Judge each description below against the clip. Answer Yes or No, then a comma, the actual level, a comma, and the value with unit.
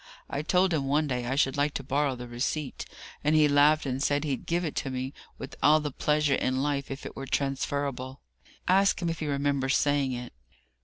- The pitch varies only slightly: Yes, narrow, 2.1 semitones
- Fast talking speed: Yes, fast, 215 wpm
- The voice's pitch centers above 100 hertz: Yes, medium, 140 Hz